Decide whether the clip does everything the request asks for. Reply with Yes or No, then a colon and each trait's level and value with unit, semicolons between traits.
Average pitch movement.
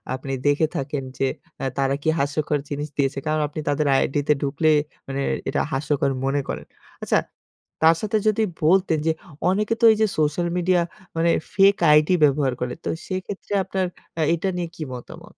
Yes: average, 4.4 semitones